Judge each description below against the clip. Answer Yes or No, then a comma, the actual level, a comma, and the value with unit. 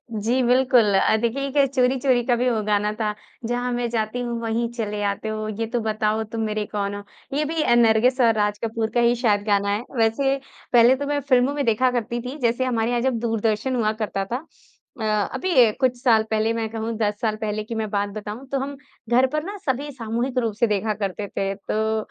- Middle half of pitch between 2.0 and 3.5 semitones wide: Yes, average, 2.7 semitones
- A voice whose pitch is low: No, high, 230 Hz